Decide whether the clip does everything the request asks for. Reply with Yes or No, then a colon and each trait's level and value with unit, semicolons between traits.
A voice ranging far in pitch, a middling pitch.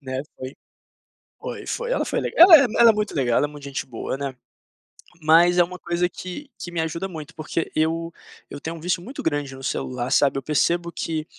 No: average, 3.9 semitones; medium, 160 Hz